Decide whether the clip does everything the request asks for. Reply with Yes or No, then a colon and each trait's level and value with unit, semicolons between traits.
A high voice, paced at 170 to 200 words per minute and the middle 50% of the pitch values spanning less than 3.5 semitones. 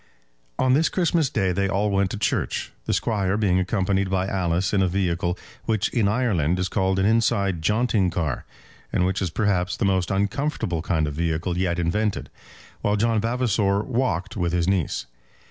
No: very low, 95 Hz; average, 180 wpm; average, 3.1 semitones